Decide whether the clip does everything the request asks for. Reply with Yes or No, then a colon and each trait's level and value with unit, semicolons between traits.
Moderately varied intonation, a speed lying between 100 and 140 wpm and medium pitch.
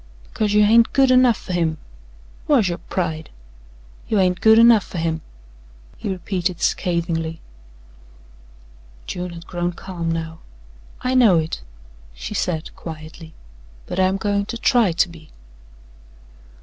Yes: average, 4.2 semitones; slow, 135 wpm; medium, 180 Hz